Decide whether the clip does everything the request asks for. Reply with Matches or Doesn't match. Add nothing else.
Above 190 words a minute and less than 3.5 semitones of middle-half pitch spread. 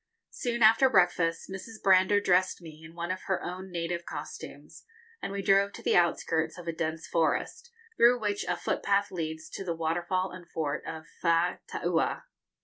Doesn't match